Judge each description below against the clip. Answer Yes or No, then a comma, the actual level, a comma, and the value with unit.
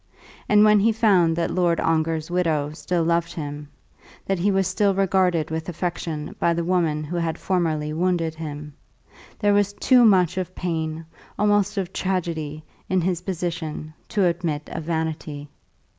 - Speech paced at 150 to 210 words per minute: Yes, average, 160 wpm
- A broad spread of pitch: No, average, 2.9 semitones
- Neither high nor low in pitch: Yes, medium, 170 Hz